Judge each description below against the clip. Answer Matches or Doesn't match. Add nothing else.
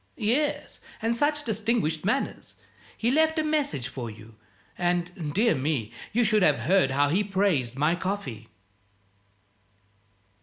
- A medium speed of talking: Doesn't match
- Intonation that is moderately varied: Doesn't match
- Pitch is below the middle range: Doesn't match